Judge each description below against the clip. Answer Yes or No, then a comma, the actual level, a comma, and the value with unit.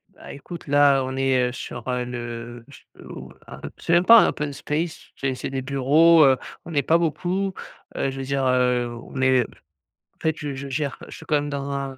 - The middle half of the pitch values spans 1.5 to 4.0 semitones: Yes, average, 2.7 semitones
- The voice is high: No, medium, 140 Hz